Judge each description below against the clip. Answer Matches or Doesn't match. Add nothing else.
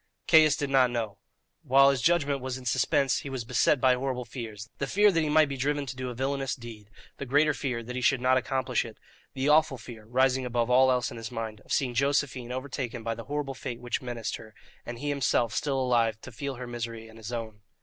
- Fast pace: Matches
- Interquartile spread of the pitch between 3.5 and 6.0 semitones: Doesn't match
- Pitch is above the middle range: Doesn't match